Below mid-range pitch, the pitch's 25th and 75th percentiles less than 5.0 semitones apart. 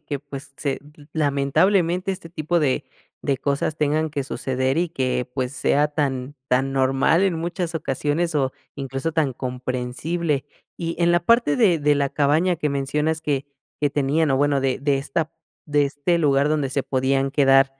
No: medium, 145 Hz; average, 3.0 semitones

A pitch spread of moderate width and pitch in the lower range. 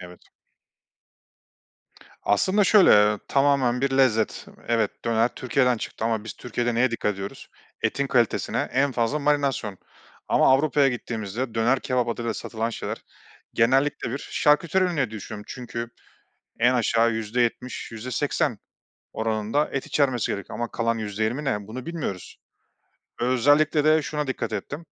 Yes: average, 3.7 semitones; low, 120 Hz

